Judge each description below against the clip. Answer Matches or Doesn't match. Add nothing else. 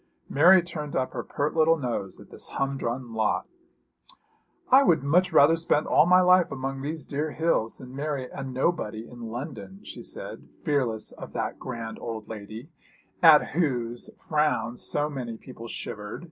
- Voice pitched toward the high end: Doesn't match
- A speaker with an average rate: Matches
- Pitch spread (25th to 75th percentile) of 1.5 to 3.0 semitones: Doesn't match